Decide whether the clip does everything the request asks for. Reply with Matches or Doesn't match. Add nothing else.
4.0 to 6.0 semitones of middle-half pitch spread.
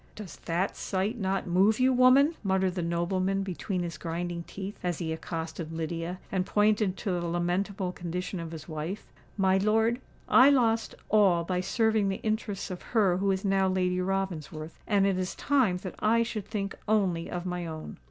Doesn't match